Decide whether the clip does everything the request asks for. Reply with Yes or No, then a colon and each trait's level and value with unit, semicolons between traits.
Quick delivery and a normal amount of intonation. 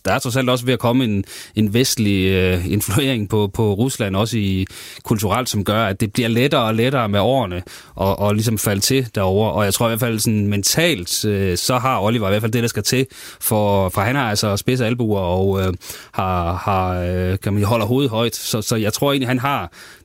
Yes: fast, 230 wpm; average, 3.8 semitones